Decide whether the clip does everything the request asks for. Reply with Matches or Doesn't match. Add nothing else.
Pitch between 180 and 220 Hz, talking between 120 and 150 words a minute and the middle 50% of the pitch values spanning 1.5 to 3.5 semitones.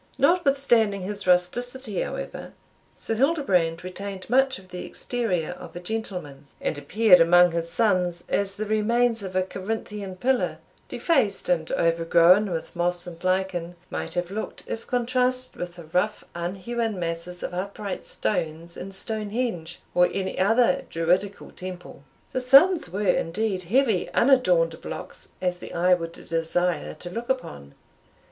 Doesn't match